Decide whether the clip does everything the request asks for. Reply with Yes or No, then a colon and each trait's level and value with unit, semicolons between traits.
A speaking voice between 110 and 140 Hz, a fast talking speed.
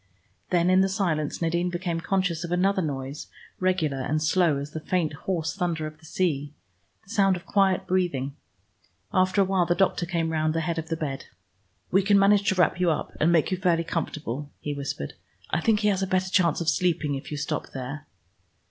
No: medium, 170 Hz; fast, 210 wpm